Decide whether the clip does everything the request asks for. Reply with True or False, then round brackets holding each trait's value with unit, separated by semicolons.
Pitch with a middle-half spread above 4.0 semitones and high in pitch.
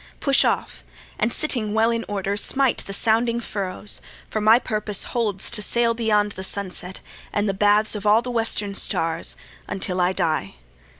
False (2.7 semitones; 210 Hz)